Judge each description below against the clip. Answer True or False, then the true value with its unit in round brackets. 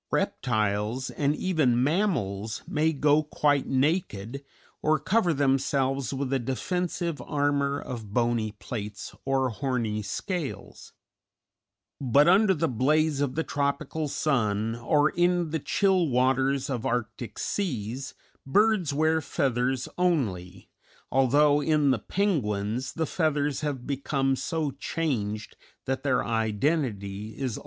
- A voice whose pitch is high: False (135 Hz)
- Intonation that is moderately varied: True (4.6 semitones)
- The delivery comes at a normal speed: False (125 wpm)